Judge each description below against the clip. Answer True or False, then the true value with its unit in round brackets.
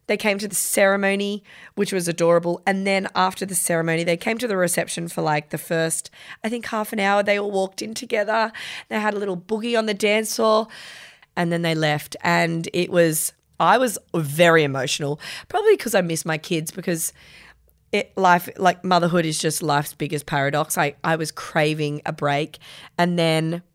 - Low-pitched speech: False (175 Hz)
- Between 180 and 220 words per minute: True (190 wpm)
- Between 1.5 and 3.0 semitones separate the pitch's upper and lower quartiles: False (3.9 semitones)